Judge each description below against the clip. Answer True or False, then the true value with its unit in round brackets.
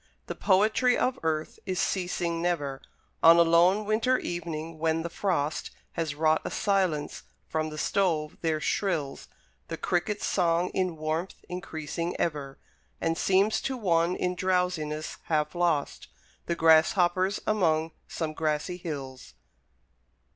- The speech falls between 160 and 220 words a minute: False (135 wpm)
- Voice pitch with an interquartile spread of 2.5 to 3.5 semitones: True (2.8 semitones)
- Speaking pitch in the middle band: True (170 Hz)